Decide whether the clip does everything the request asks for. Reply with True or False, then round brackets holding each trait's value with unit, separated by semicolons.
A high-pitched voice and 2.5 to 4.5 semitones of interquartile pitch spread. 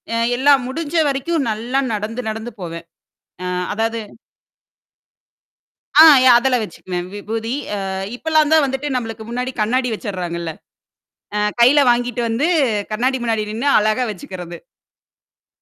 True (235 Hz; 3.7 semitones)